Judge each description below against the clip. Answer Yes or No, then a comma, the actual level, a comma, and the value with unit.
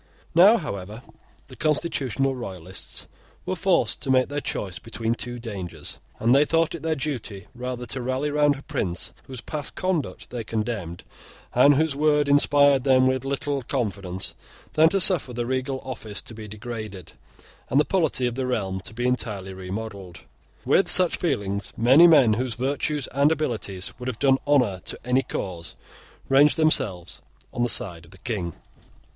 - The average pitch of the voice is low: Yes, low, 125 Hz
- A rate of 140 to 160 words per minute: No, average, 170 wpm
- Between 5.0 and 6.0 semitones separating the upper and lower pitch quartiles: Yes, wide, 5.4 semitones